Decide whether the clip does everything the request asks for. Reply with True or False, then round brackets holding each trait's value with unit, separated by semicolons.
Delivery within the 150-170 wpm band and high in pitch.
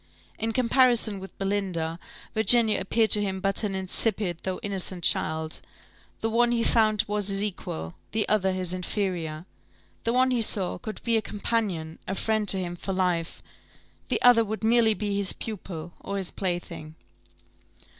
True (165 wpm; 200 Hz)